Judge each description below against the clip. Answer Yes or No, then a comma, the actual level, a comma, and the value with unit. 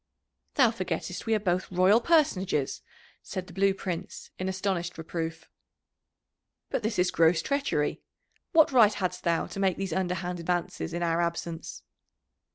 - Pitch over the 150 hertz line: Yes, medium, 185 Hz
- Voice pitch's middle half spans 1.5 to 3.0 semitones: Yes, narrow, 2.6 semitones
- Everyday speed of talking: Yes, average, 150 wpm